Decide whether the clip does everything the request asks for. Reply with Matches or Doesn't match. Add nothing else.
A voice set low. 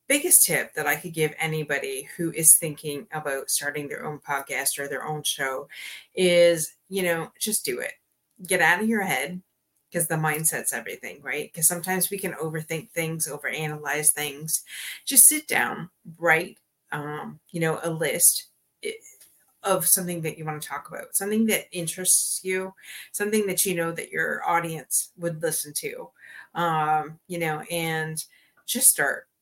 Doesn't match